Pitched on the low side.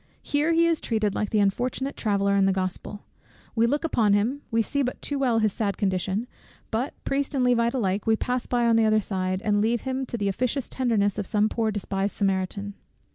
No: high, 220 Hz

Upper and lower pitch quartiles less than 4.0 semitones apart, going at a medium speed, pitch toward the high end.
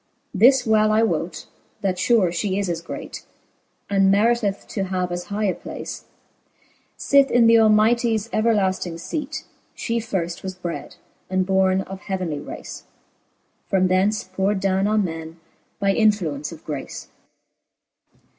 Yes: average, 2.9 semitones; average, 145 wpm; high, 195 Hz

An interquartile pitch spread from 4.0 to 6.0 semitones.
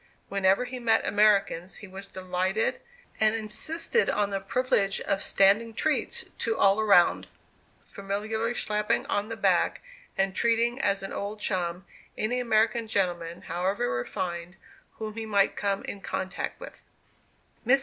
No: narrow, 2.6 semitones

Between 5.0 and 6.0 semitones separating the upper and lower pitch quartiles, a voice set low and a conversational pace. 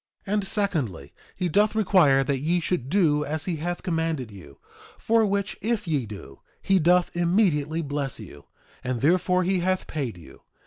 No: wide, 5.6 semitones; medium, 165 Hz; average, 175 wpm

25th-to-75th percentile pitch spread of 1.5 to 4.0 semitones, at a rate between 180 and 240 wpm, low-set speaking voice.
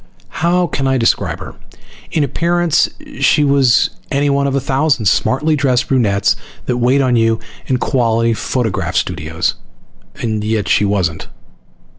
No: average, 3.7 semitones; average, 140 wpm; low, 130 Hz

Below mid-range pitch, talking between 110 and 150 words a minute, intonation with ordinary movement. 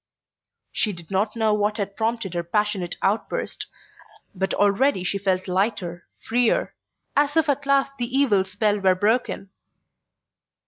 No: high, 210 Hz; average, 140 wpm; average, 3.9 semitones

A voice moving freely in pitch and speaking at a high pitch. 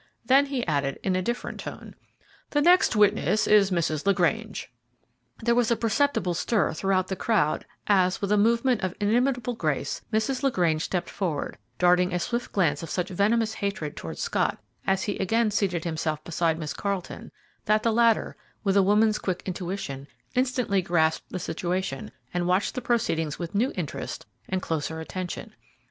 No: average, 4.7 semitones; high, 195 Hz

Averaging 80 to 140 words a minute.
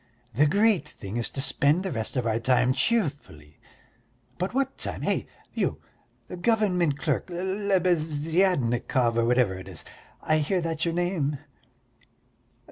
Yes: slow, 135 wpm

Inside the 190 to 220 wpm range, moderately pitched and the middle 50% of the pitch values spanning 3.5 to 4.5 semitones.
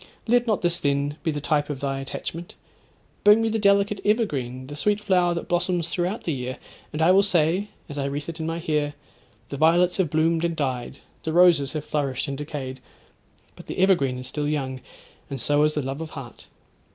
Yes: fast, 205 wpm; medium, 155 Hz; average, 4.1 semitones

